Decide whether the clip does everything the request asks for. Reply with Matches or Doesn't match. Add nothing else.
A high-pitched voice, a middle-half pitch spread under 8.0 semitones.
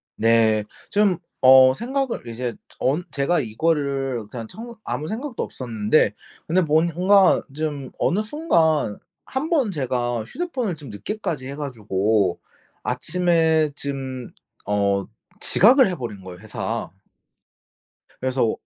Doesn't match